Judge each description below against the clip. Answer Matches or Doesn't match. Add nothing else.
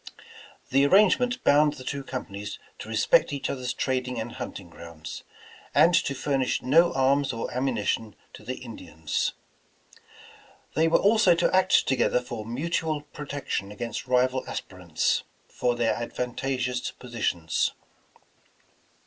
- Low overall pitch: Matches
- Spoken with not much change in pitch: Doesn't match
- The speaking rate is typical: Doesn't match